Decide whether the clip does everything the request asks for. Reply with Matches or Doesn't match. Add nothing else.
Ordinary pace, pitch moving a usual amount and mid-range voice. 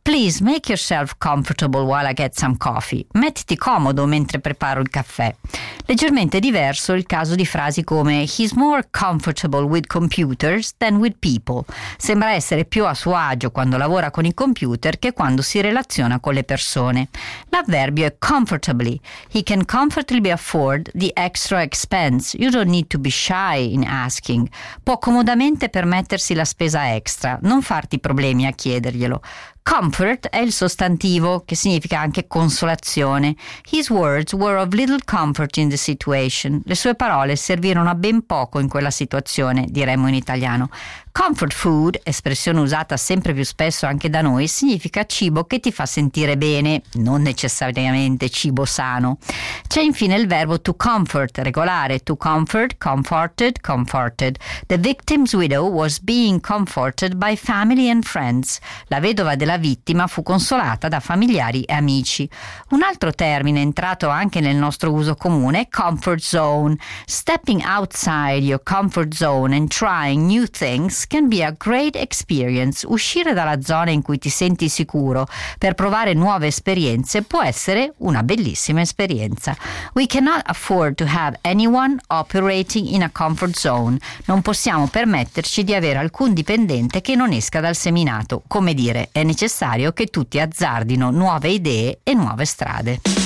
Doesn't match